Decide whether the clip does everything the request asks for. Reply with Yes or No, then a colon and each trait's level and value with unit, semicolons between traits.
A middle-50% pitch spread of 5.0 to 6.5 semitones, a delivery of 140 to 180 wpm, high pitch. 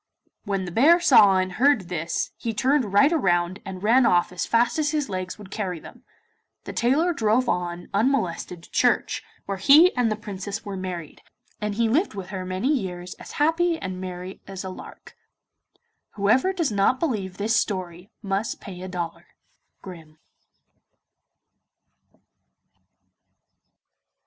Yes: average, 5.3 semitones; average, 150 wpm; high, 200 Hz